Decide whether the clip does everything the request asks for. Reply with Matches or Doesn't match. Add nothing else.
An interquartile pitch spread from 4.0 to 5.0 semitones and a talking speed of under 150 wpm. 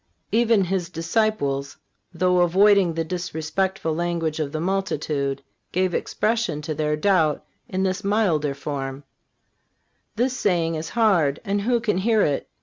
Matches